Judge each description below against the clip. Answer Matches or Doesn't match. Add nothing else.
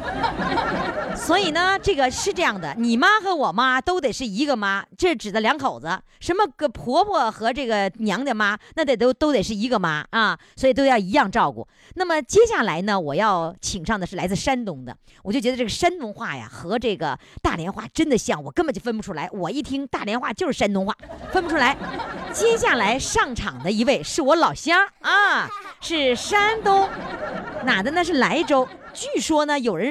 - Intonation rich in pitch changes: Matches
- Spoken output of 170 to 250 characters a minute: Doesn't match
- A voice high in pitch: Matches